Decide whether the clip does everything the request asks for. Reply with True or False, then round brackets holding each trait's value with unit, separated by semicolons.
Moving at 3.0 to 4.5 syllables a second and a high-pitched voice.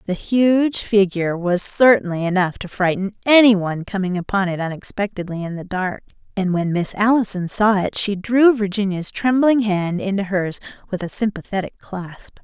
False (4.9 syllables/s; 195 Hz)